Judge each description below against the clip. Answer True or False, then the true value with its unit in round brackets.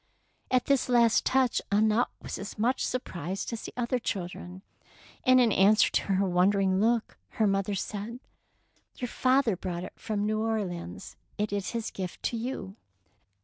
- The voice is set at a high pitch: True (210 Hz)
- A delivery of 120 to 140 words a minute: False (165 wpm)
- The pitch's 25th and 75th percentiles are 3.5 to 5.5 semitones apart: True (3.8 semitones)